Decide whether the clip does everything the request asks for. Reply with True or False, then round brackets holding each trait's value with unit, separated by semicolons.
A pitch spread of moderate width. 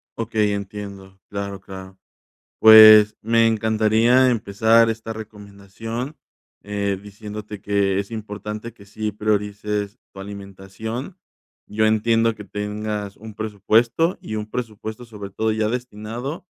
False (1.7 semitones)